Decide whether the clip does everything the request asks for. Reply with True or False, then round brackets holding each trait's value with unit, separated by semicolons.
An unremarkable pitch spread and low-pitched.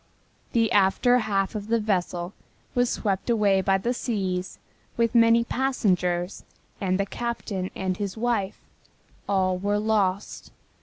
False (3.4 semitones; 200 Hz)